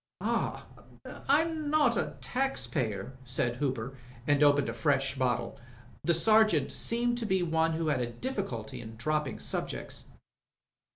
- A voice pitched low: No, medium, 150 Hz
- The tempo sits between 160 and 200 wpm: No, average, 140 wpm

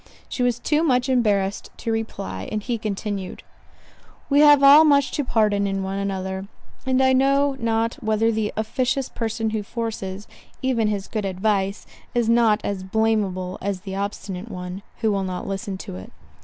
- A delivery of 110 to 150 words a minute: No, average, 170 wpm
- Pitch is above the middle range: Yes, high, 215 Hz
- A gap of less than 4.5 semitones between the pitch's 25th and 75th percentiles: Yes, average, 3.7 semitones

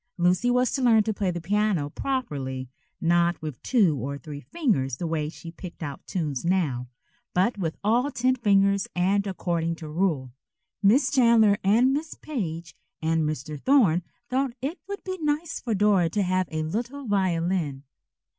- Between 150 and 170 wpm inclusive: Yes, average, 165 wpm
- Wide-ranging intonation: Yes, wide, 6.8 semitones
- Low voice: No, medium, 185 Hz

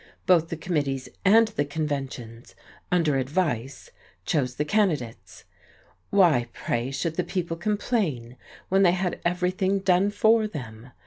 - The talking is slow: Yes, slow, 130 wpm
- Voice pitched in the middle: Yes, medium, 165 Hz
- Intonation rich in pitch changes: Yes, wide, 5.8 semitones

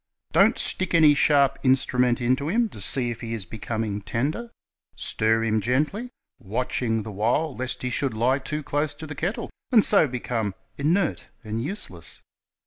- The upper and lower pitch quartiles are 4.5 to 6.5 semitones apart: Yes, average, 5.0 semitones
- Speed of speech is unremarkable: Yes, average, 170 wpm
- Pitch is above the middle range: No, low, 130 Hz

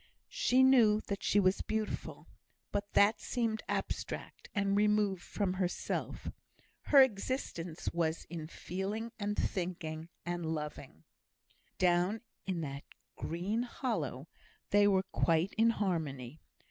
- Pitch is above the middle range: Yes, high, 195 Hz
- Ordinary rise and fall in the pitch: Yes, average, 4.2 semitones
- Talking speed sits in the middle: No, slow, 120 wpm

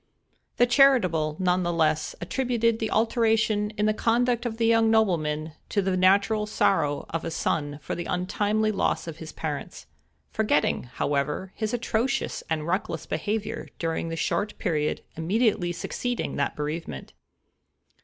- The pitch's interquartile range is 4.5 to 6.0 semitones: Yes, wide, 5.5 semitones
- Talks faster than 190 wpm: No, slow, 135 wpm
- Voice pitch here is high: Yes, high, 195 Hz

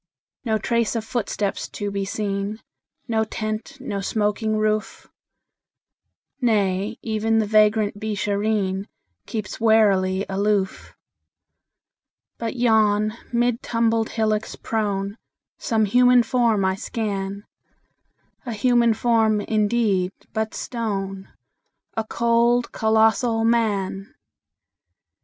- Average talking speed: No, slow, 95 wpm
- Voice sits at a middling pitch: No, high, 215 Hz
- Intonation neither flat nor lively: No, narrow, 2.1 semitones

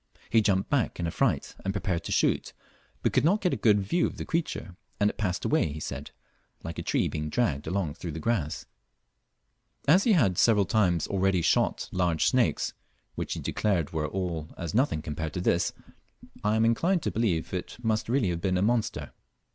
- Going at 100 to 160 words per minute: No, average, 200 wpm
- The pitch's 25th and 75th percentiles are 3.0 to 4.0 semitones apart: No, average, 5.2 semitones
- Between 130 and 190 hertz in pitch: No, very low, 95 Hz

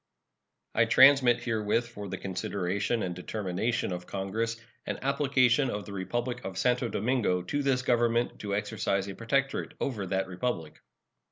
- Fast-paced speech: No, average, 150 wpm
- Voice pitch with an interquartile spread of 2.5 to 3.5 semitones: No, average, 4.3 semitones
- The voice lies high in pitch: No, low, 115 Hz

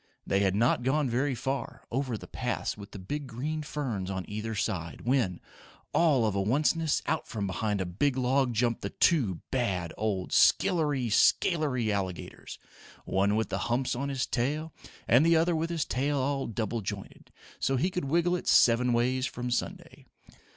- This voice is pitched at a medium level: No, low, 125 Hz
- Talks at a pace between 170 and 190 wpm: Yes, average, 180 wpm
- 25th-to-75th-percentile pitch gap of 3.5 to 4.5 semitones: No, wide, 5.4 semitones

